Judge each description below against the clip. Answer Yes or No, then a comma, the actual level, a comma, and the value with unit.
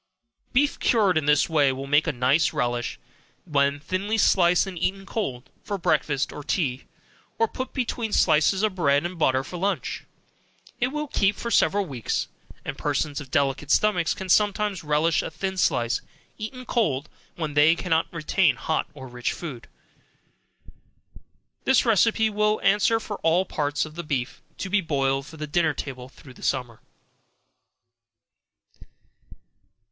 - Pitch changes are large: Yes, wide, 6.2 semitones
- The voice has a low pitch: No, medium, 165 Hz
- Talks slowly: No, average, 155 wpm